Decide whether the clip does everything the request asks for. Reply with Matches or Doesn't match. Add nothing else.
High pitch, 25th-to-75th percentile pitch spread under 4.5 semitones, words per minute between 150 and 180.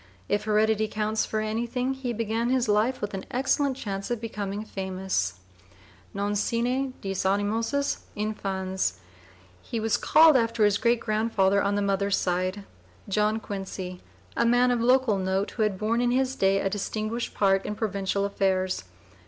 Matches